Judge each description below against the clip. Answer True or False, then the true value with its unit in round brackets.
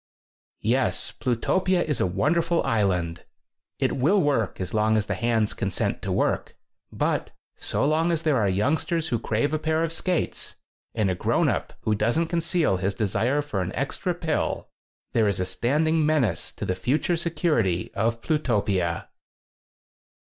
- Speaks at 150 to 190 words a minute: True (165 wpm)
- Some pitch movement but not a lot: False (7.6 semitones)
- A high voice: False (125 Hz)